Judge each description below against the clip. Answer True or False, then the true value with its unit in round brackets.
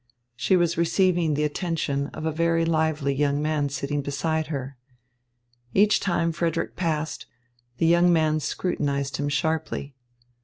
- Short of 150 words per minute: True (140 wpm)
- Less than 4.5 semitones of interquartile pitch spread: True (2.7 semitones)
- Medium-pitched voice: True (155 Hz)